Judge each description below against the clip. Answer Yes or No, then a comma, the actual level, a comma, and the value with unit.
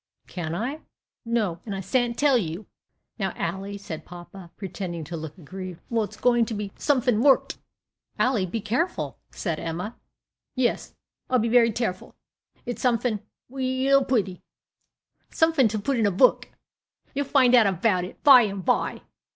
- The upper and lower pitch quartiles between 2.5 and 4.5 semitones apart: No, average, 5.2 semitones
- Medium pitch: No, high, 220 Hz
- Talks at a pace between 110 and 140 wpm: No, average, 160 wpm